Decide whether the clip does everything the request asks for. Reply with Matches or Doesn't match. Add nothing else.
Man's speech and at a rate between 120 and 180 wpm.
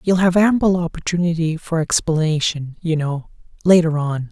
Matches